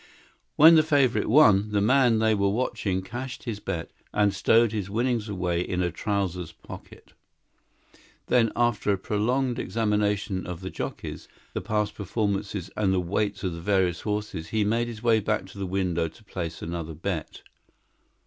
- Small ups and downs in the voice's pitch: No, average, 3.3 semitones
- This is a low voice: Yes, low, 105 Hz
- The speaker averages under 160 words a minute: No, average, 170 wpm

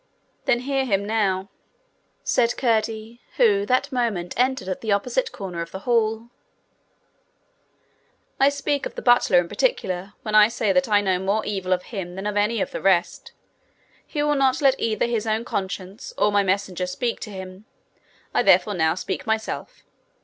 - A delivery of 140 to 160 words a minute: No, average, 175 wpm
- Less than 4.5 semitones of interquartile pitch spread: Yes, average, 4.1 semitones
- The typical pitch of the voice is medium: No, high, 215 Hz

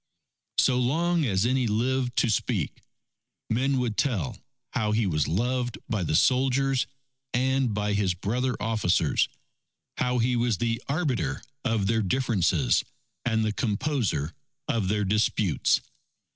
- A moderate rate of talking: No, slow, 130 wpm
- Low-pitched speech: Yes, low, 115 Hz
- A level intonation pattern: No, average, 3.8 semitones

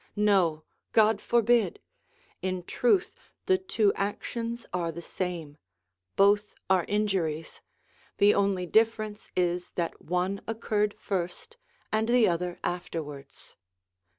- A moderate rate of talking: No, slow, 110 wpm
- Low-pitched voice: No, high, 195 Hz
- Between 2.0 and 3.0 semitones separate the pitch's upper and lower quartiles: No, average, 3.8 semitones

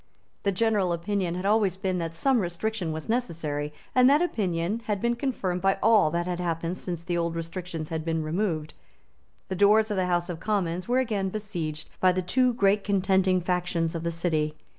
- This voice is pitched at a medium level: Yes, medium, 180 Hz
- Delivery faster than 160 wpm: Yes, average, 195 wpm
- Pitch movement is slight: No, average, 3.8 semitones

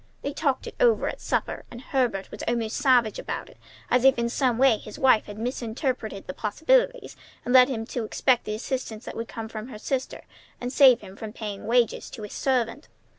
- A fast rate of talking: Yes, fast, 210 wpm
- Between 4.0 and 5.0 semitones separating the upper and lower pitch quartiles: No, average, 3.2 semitones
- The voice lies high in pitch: Yes, high, 240 Hz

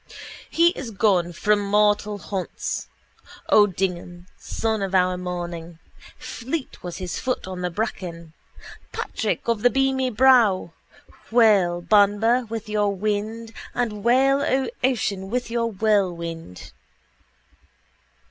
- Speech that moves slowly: Yes, slow, 115 wpm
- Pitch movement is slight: No, average, 4.2 semitones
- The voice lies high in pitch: Yes, high, 210 Hz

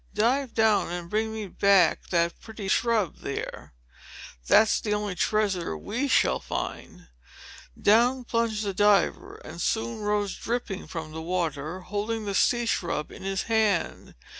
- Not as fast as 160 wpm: Yes, average, 145 wpm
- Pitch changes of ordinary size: Yes, average, 3.6 semitones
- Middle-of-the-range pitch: No, high, 205 Hz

